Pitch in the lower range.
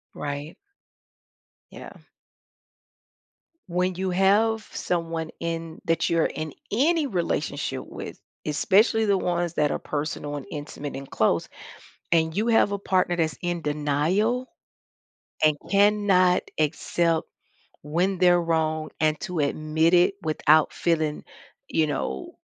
No: medium, 165 Hz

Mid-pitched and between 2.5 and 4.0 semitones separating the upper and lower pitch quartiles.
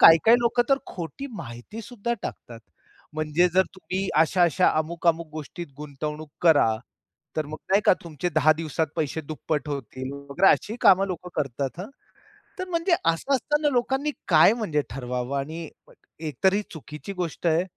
No: medium, 165 Hz; average, 4.7 semitones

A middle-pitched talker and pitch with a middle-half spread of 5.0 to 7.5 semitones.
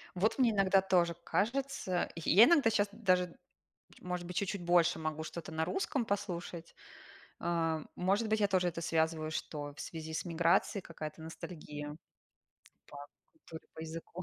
No: medium, 175 Hz; average, 3.8 semitones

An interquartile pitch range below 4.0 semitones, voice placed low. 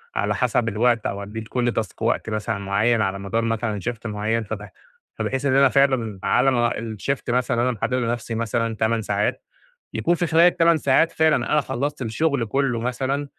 Yes: average, 3.6 semitones; low, 120 Hz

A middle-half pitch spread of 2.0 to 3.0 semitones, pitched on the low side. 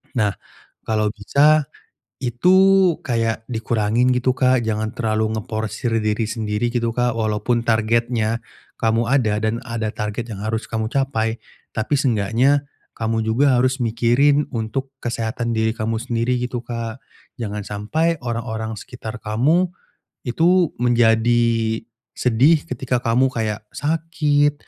Yes: narrow, 2.4 semitones; low, 115 Hz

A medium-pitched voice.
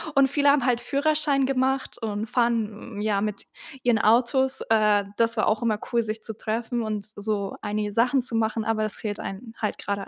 No: high, 225 Hz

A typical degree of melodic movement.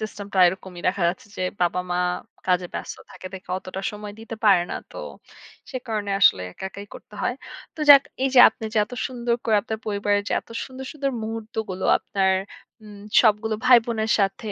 Yes: average, 3.0 semitones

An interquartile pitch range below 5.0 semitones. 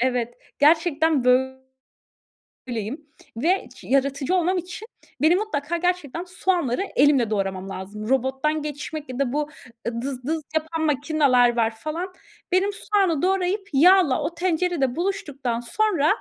No: wide, 5.5 semitones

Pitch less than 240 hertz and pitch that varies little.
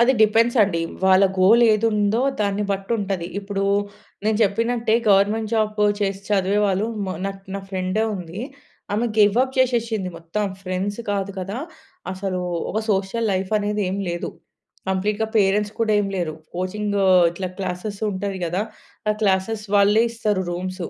Yes: high, 200 Hz; narrow, 2.0 semitones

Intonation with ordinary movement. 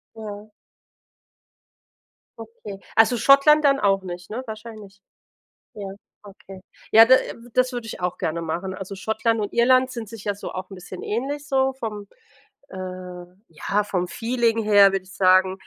Yes: average, 3.6 semitones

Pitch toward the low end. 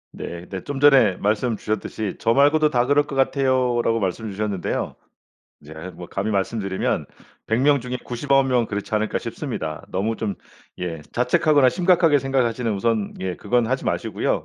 Yes: low, 115 Hz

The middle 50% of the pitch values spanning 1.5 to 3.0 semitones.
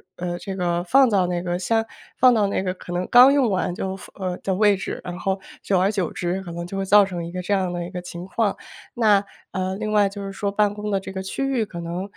Yes: narrow, 2.5 semitones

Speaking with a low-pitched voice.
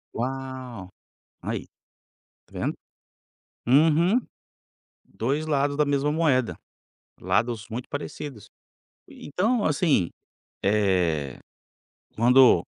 Yes: low, 130 Hz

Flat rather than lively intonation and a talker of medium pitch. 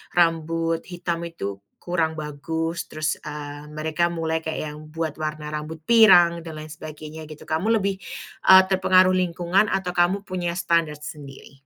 Yes: narrow, 2.3 semitones; medium, 165 Hz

